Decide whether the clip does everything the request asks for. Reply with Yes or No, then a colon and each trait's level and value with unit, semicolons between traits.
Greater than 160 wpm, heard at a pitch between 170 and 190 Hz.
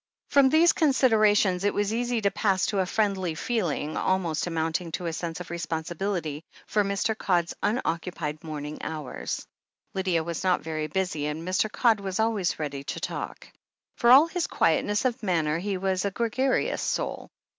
Yes: average, 170 wpm; medium, 185 Hz